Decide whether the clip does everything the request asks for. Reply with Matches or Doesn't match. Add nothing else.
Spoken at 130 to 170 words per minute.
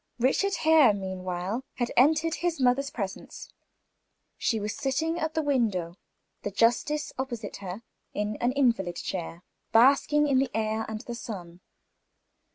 Matches